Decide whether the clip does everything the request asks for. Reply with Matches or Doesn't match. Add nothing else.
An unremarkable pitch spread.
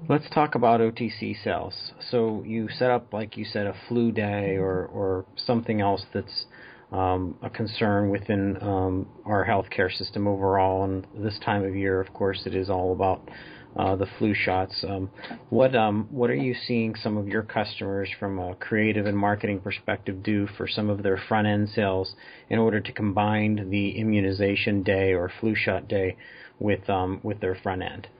Doesn't match